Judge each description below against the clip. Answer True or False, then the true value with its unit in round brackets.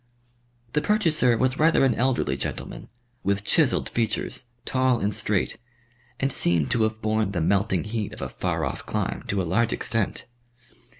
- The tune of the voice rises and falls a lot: False (4.3 semitones)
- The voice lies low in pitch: True (110 Hz)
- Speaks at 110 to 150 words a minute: False (165 wpm)